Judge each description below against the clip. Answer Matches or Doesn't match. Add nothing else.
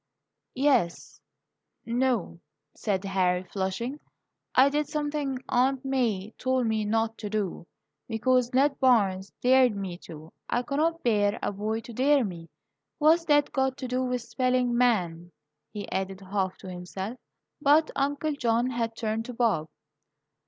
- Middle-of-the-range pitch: Doesn't match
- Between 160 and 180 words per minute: Doesn't match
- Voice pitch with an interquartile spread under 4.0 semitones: Doesn't match